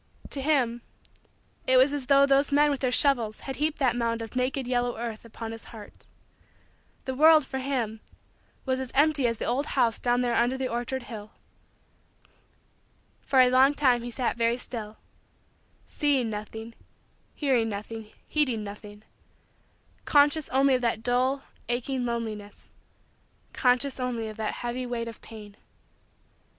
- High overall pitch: Yes, high, 245 Hz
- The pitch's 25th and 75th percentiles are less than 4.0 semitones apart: Yes, average, 2.9 semitones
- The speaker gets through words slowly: No, average, 155 wpm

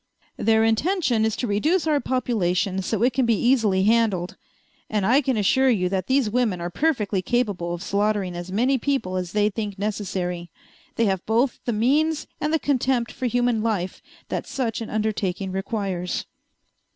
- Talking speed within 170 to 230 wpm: Yes, average, 175 wpm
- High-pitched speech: Yes, high, 220 Hz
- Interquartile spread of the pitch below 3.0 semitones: No, average, 4.6 semitones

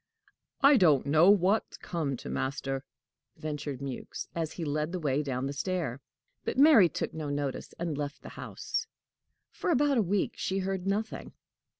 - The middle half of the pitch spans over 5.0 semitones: Yes, wide, 5.4 semitones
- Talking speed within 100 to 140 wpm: No, average, 170 wpm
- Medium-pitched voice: Yes, medium, 160 Hz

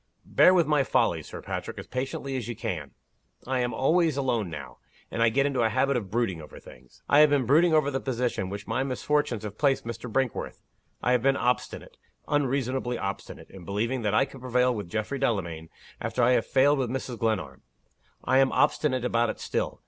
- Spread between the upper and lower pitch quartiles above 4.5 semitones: No, average, 3.7 semitones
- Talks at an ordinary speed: No, fast, 210 wpm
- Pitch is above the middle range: No, low, 125 Hz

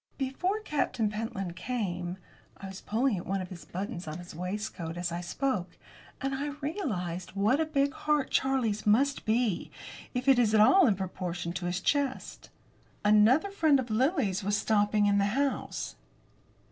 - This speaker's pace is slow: No, average, 170 wpm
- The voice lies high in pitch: Yes, high, 215 Hz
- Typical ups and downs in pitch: No, wide, 6.5 semitones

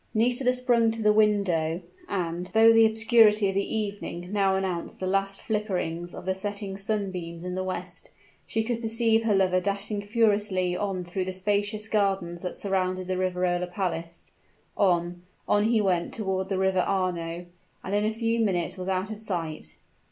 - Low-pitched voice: No, high, 195 Hz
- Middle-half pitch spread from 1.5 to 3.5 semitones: Yes, average, 2.7 semitones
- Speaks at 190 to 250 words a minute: No, average, 175 wpm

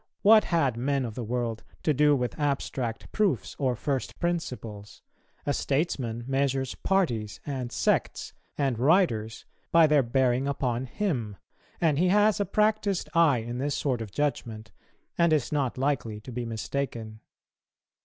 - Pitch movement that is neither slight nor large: Yes, average, 4.7 semitones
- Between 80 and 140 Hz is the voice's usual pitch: Yes, low, 135 Hz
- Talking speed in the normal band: Yes, average, 150 wpm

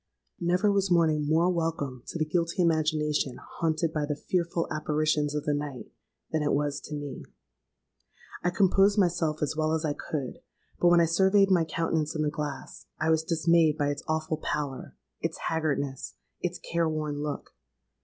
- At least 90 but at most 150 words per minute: No, average, 165 wpm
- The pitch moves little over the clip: Yes, narrow, 2.2 semitones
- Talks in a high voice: No, medium, 155 Hz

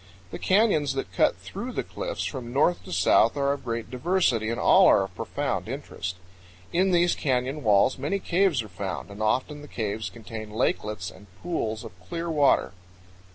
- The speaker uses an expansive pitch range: Yes, wide, 6.8 semitones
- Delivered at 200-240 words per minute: No, average, 180 wpm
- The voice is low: Yes, low, 130 Hz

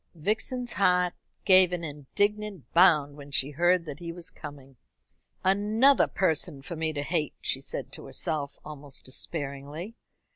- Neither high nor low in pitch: Yes, medium, 165 Hz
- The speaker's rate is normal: Yes, average, 145 wpm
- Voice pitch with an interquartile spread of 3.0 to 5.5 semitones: Yes, average, 4.4 semitones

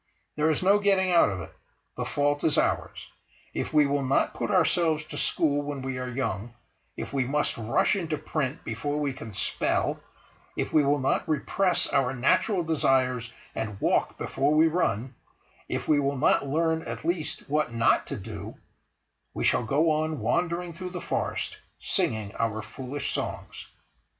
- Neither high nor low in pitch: Yes, medium, 145 Hz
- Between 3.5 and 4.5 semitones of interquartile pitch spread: Yes, average, 3.9 semitones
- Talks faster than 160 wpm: Yes, average, 170 wpm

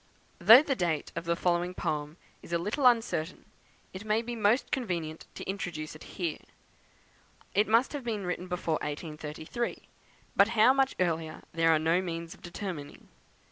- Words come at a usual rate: Yes, average, 165 wpm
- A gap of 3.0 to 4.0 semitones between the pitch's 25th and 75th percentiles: No, average, 5.2 semitones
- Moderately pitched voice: Yes, medium, 180 Hz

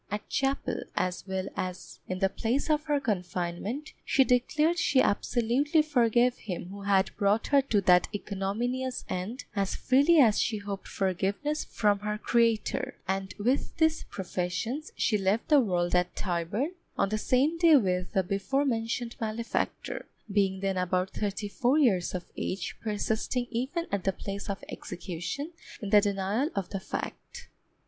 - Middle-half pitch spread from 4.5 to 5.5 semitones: Yes, average, 5.2 semitones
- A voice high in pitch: Yes, high, 210 Hz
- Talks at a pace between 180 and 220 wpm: No, average, 160 wpm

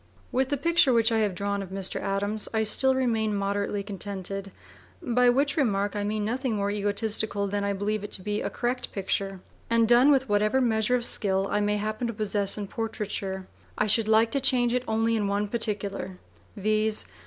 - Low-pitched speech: No, high, 215 Hz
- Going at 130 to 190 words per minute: No, average, 200 wpm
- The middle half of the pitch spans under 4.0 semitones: Yes, narrow, 2.5 semitones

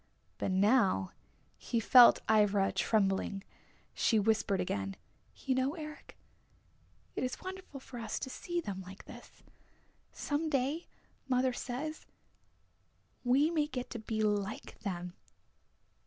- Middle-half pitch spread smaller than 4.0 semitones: No, wide, 5.6 semitones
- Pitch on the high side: Yes, high, 240 Hz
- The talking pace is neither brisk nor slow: No, slow, 125 wpm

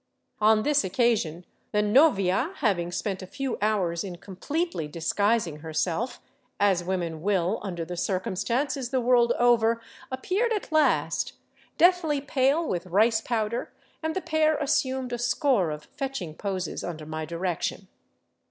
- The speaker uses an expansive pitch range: Yes, wide, 6.9 semitones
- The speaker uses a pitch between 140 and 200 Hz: No, high, 215 Hz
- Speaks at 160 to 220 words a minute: No, average, 145 wpm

